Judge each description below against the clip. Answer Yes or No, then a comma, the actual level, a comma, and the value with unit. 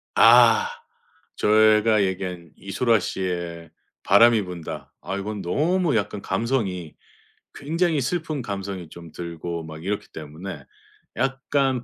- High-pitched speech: No, low, 100 Hz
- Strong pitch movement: Yes, wide, 6.1 semitones